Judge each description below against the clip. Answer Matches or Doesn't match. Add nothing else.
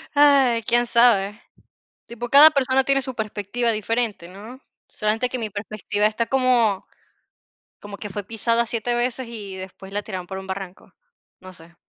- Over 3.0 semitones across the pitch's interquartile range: Matches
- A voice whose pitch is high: Matches